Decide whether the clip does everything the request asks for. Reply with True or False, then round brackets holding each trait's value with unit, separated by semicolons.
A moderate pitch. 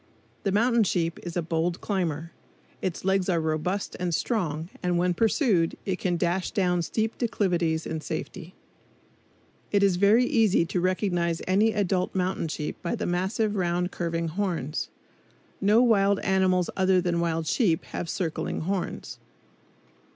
True (180 Hz)